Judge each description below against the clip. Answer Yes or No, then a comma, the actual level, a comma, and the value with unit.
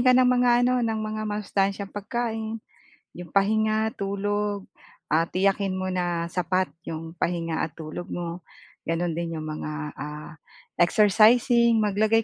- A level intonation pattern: No, average, 4.3 semitones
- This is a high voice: Yes, high, 195 Hz